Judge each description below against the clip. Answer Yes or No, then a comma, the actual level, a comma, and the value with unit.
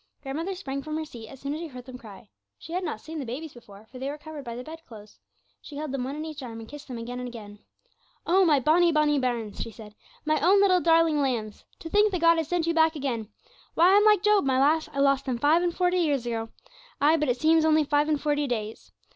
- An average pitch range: Yes, average, 4.6 semitones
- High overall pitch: Yes, very high, 290 Hz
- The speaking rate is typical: No, fast, 265 wpm